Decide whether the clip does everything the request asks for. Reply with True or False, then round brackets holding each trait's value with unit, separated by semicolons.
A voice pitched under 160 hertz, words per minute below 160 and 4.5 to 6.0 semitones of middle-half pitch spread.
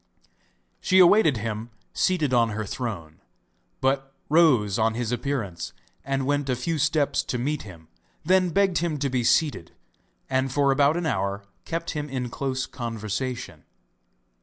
True (135 Hz; 150 wpm; 4.8 semitones)